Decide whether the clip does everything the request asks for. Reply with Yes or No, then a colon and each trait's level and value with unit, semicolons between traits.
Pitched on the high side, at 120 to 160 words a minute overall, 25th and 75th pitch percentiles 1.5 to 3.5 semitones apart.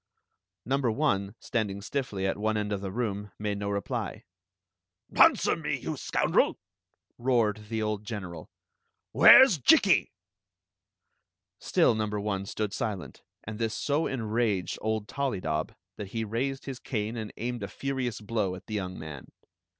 No: low, 105 Hz; average, 155 wpm; average, 2.9 semitones